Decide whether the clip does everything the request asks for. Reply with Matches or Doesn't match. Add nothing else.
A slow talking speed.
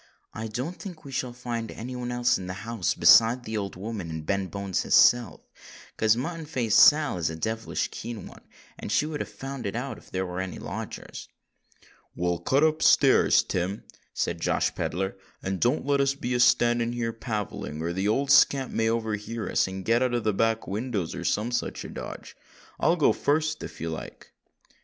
Doesn't match